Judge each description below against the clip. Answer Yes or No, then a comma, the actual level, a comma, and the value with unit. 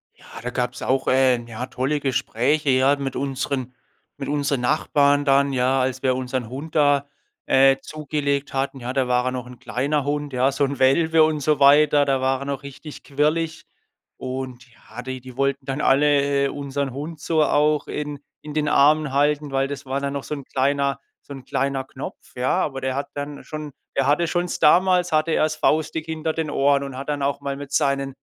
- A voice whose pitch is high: No, medium, 140 Hz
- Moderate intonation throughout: No, narrow, 1.9 semitones